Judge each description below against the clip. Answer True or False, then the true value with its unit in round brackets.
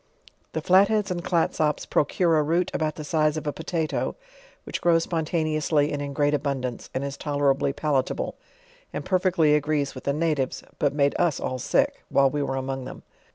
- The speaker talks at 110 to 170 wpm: False (185 wpm)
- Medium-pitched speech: True (150 Hz)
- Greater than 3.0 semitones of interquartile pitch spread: False (2.7 semitones)